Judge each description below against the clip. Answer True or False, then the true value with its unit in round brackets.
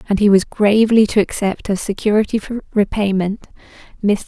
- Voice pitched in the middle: False (205 Hz)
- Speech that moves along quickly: False (140 wpm)